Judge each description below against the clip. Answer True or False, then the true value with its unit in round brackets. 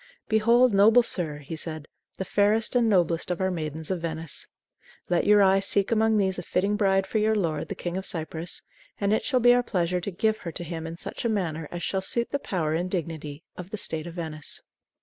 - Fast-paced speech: True (230 wpm)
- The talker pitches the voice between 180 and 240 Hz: True (185 Hz)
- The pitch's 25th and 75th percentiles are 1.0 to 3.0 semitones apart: False (4.3 semitones)